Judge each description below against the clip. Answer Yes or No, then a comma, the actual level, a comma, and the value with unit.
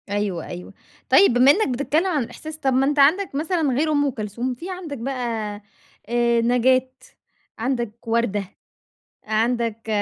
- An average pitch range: Yes, average, 4.1 semitones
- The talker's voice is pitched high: Yes, very high, 250 Hz